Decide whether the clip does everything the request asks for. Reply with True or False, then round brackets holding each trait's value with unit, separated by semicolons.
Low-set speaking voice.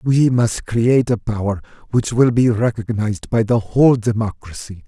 True (115 Hz)